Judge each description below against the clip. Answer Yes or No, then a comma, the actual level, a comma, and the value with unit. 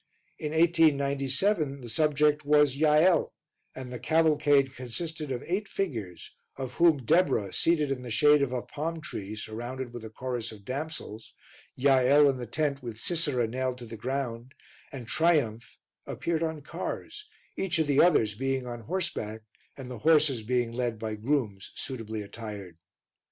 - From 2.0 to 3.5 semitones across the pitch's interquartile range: No, average, 4.6 semitones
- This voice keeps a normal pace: Yes, average, 155 wpm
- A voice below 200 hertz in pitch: Yes, low, 135 Hz